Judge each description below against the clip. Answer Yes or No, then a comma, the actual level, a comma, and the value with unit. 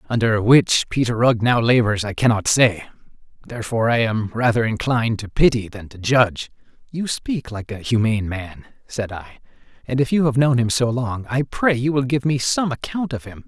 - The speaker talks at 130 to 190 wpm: No, average, 200 wpm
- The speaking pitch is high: No, low, 120 Hz